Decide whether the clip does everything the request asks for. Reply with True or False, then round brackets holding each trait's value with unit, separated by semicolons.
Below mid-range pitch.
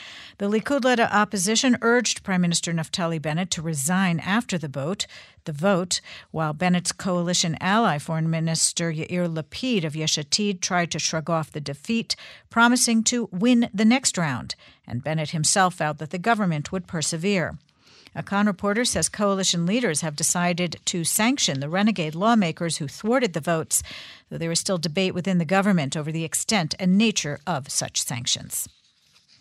False (180 Hz)